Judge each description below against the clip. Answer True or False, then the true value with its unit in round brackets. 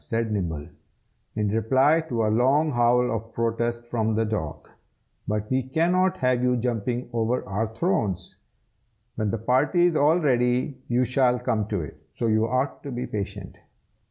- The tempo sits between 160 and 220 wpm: True (165 wpm)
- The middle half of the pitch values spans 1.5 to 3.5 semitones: True (2.9 semitones)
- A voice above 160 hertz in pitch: False (120 Hz)